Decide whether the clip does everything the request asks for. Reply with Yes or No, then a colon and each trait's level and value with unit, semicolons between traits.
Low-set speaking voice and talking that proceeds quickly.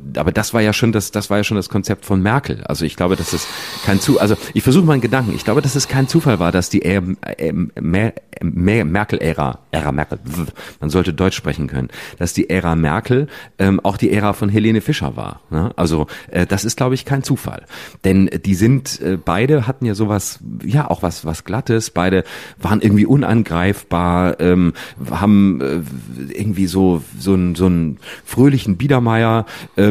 Yes: low, 100 Hz; fast, 195 wpm